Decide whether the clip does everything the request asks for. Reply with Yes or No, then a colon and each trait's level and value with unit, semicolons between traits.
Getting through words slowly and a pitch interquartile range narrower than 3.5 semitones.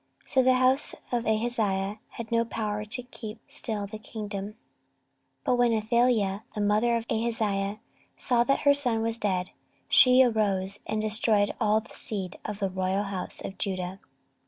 No: average, 165 wpm; average, 2.8 semitones